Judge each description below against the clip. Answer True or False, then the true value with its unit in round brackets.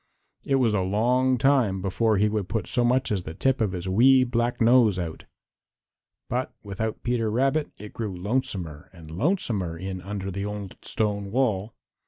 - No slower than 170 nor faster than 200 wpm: True (175 wpm)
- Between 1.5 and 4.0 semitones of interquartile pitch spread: False (4.5 semitones)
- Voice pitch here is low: True (105 Hz)